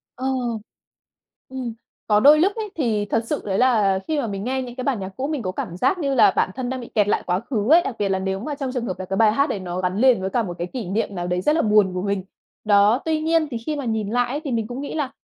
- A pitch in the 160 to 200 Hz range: No, high, 230 Hz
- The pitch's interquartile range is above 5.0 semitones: Yes, wide, 5.4 semitones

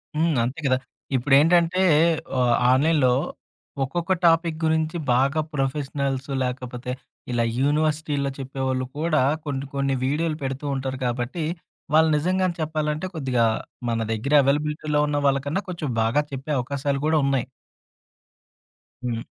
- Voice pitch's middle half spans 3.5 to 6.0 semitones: No, average, 3.0 semitones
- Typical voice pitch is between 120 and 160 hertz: Yes, medium, 140 Hz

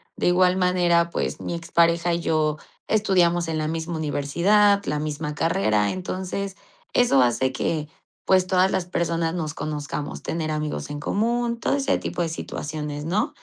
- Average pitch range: Yes, average, 3.3 semitones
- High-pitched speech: No, medium, 170 Hz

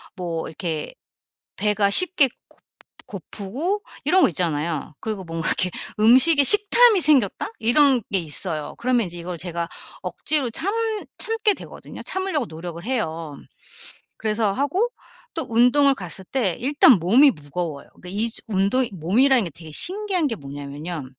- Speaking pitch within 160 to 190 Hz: No, high, 210 Hz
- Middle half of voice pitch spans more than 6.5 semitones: Yes, wide, 8.7 semitones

